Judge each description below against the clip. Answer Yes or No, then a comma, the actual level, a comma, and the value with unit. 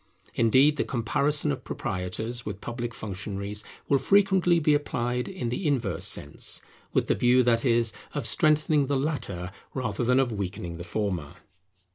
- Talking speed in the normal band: Yes, average, 155 wpm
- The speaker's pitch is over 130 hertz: No, low, 120 Hz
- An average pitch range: No, wide, 5.7 semitones